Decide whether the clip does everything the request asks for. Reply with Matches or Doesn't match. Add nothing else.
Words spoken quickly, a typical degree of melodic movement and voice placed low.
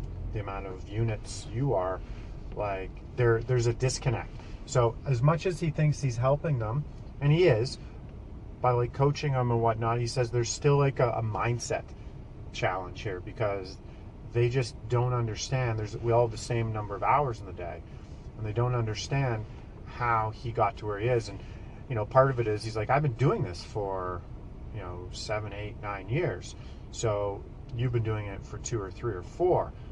Doesn't match